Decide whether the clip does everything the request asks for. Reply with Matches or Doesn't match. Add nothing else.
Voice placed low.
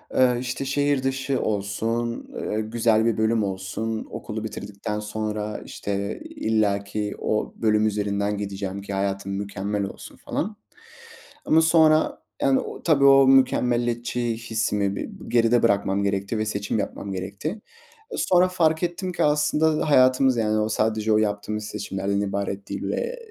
Matches